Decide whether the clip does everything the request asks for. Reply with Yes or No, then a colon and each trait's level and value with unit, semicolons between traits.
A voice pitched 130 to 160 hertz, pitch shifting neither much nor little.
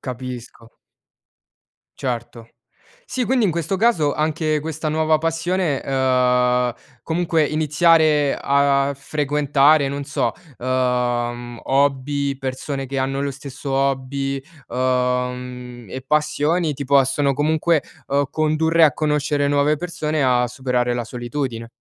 Yes: medium, 140 Hz; average, 3.2 semitones